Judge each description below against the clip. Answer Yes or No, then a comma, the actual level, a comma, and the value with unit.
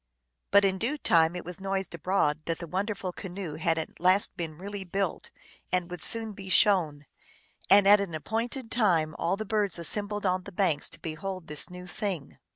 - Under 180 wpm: No, average, 190 wpm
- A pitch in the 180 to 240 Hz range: Yes, medium, 185 Hz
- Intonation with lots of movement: No, average, 3.2 semitones